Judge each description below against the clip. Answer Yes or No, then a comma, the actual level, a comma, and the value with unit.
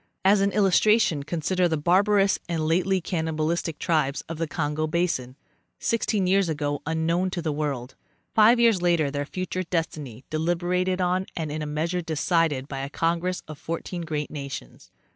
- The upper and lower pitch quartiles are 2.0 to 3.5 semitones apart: Yes, average, 3.2 semitones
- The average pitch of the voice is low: No, medium, 165 Hz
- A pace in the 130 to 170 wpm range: Yes, average, 165 wpm